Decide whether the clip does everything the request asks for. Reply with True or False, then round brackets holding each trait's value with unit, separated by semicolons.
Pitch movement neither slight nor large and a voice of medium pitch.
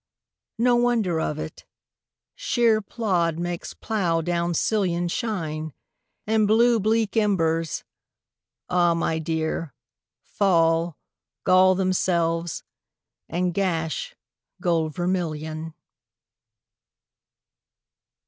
True (3.8 semitones; 175 Hz)